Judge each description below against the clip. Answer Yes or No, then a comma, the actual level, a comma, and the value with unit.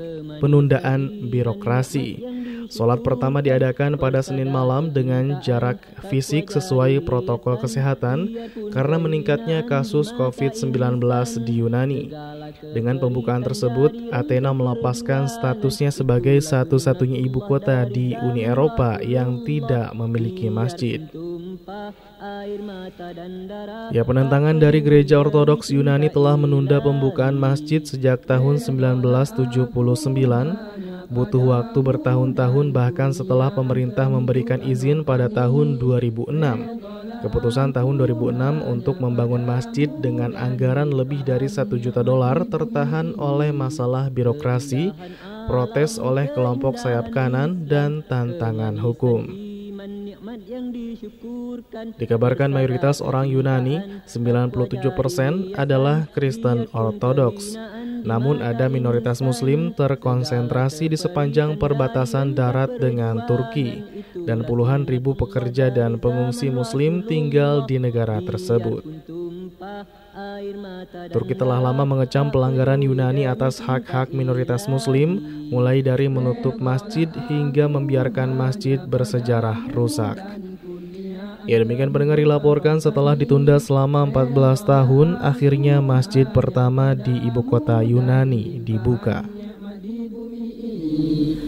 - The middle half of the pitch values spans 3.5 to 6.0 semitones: No, average, 3.1 semitones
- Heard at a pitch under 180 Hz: Yes, low, 135 Hz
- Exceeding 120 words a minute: No, average, 100 wpm